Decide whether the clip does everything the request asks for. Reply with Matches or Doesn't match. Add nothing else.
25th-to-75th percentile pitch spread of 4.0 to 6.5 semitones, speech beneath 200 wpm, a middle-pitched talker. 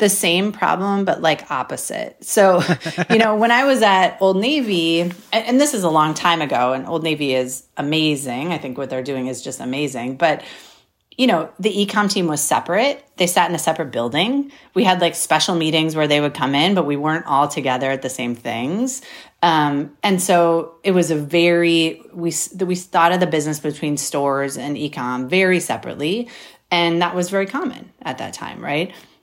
Doesn't match